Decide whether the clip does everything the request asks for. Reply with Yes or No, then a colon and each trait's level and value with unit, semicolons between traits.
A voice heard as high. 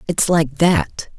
No: medium, 160 Hz